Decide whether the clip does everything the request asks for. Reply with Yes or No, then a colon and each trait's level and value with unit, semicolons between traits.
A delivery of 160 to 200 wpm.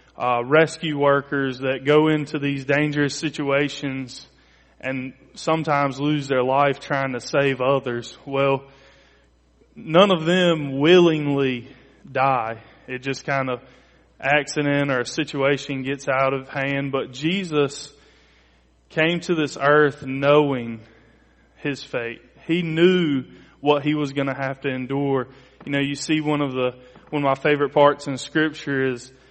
No: average, 145 wpm